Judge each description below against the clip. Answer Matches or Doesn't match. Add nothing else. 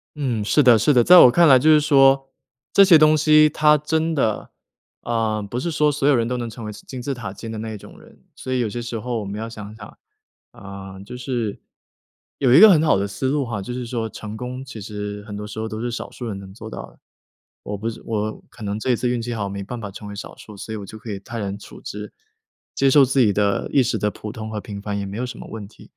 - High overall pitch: Doesn't match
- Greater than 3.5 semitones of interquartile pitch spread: Matches